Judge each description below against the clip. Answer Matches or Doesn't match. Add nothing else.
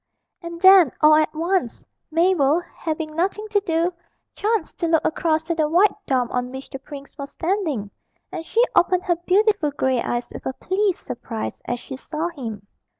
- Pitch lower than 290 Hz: Doesn't match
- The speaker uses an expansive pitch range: Doesn't match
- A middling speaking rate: Matches